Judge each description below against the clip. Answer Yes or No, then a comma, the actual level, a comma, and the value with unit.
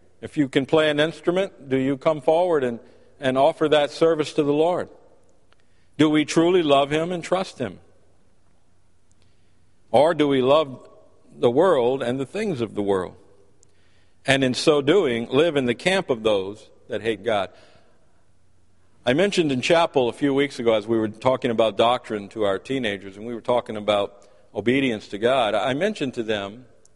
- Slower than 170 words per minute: No, average, 180 wpm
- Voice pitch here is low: Yes, low, 120 Hz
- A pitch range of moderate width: No, wide, 7.3 semitones